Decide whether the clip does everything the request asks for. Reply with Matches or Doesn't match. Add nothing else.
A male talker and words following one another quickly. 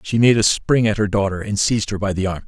Matches